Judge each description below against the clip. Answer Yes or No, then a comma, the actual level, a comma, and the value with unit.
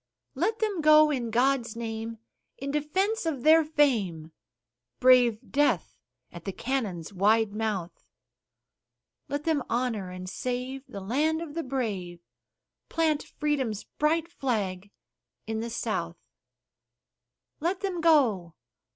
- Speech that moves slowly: Yes, slow, 120 wpm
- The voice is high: Yes, very high, 255 Hz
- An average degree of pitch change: No, wide, 6.1 semitones